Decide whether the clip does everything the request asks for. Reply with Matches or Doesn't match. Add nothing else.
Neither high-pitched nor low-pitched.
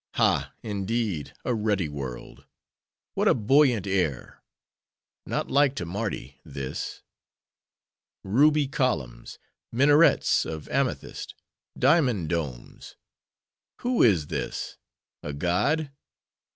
Doesn't match